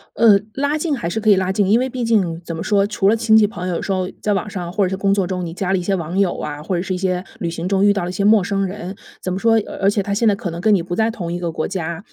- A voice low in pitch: No, high, 195 Hz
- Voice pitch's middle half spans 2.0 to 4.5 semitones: Yes, average, 2.8 semitones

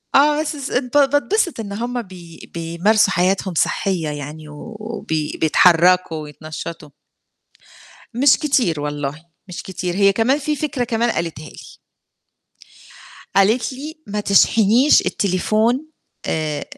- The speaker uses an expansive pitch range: Yes, wide, 7.1 semitones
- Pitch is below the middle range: No, high, 200 Hz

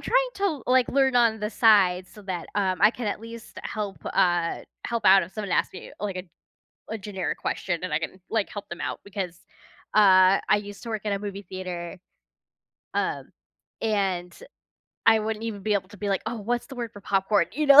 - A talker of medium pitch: No, high, 205 Hz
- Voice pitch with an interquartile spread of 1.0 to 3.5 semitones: Yes, average, 3.1 semitones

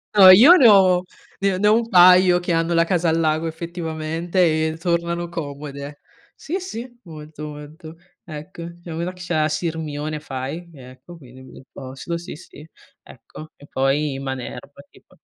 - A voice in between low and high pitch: Yes, medium, 165 Hz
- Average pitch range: Yes, average, 3.1 semitones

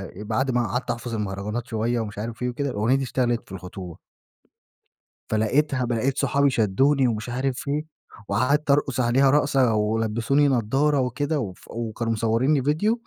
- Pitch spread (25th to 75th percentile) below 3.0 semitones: No, average, 3.8 semitones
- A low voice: Yes, low, 120 Hz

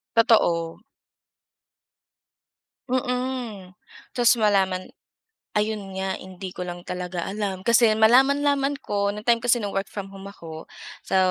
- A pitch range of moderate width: Yes, average, 4.0 semitones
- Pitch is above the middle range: Yes, high, 205 Hz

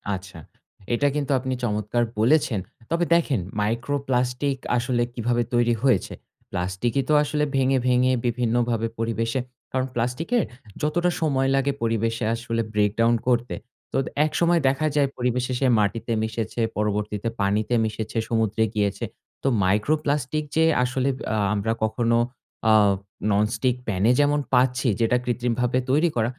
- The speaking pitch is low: Yes, low, 120 Hz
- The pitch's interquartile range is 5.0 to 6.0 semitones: No, average, 3.1 semitones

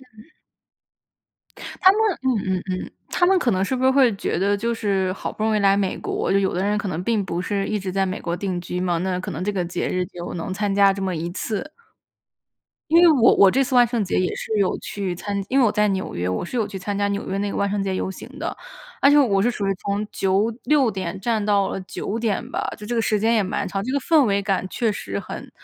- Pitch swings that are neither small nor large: Yes, average, 3.3 semitones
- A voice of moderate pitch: No, high, 200 Hz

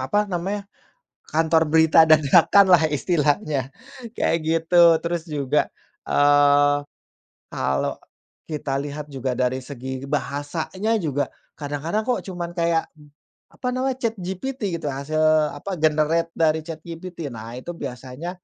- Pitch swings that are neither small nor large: Yes, average, 3.3 semitones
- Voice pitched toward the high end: No, medium, 155 Hz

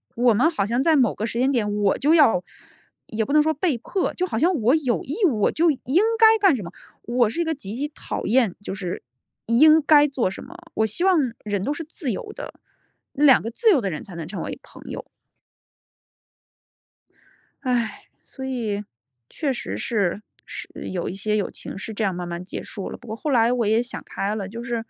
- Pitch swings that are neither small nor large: No, wide, 6.0 semitones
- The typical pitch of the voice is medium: No, high, 235 Hz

